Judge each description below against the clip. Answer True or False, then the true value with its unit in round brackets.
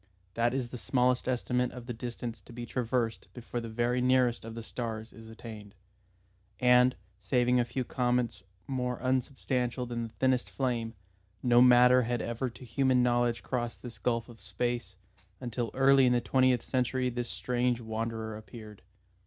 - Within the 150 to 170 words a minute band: True (165 wpm)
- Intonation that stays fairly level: True (1.4 semitones)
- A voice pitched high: False (120 Hz)